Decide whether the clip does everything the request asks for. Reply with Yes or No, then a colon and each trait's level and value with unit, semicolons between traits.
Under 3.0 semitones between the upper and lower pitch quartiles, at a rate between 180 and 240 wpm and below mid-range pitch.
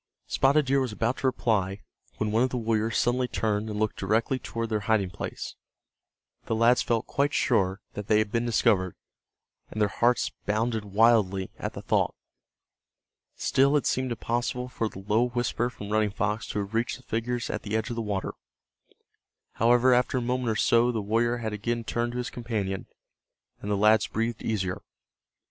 Yes: narrow, 2.5 semitones; average, 185 wpm; low, 115 Hz